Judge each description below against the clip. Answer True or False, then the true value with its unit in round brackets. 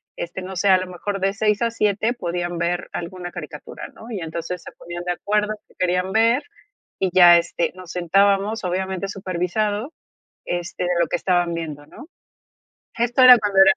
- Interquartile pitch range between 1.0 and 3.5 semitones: True (2.9 semitones)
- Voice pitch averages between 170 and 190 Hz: True (185 Hz)